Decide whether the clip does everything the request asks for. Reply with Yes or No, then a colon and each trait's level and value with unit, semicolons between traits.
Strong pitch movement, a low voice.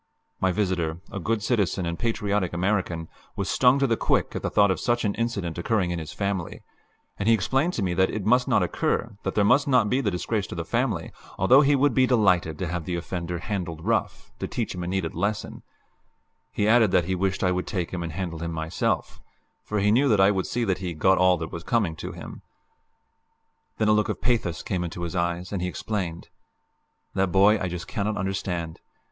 No: average, 3.7 semitones; very low, 95 Hz